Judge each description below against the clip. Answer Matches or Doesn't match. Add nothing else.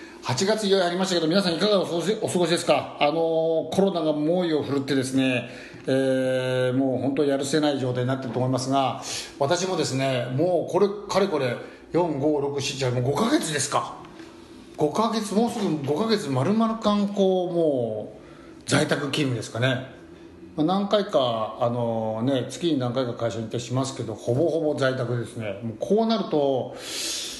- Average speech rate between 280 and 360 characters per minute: Matches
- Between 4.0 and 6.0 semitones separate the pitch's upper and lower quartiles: Matches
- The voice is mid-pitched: Matches